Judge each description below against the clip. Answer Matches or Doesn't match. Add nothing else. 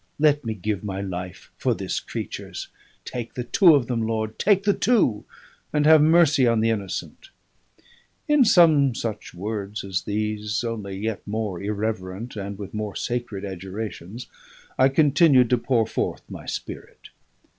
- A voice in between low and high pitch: Doesn't match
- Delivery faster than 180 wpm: Doesn't match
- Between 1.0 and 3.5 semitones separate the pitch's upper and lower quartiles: Doesn't match